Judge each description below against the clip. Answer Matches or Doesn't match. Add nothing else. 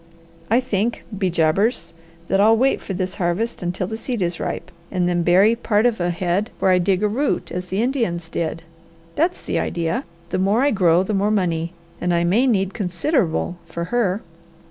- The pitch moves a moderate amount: Matches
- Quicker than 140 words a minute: Matches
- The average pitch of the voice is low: Doesn't match